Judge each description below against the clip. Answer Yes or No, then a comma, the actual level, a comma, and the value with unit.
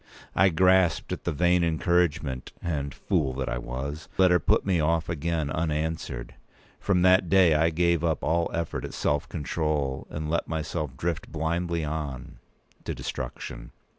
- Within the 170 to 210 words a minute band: No, average, 155 wpm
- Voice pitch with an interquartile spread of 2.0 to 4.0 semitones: Yes, average, 2.8 semitones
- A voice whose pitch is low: Yes, very low, 80 Hz